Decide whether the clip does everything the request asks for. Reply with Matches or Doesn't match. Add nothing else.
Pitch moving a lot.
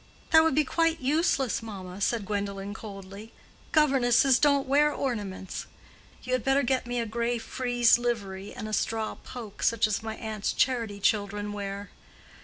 Doesn't match